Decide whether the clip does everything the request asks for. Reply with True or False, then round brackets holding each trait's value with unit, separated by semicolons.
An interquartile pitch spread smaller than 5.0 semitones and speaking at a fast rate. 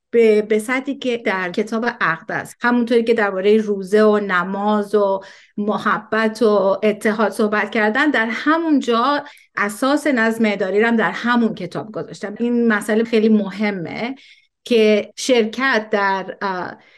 False (2.6 semitones; 130 wpm)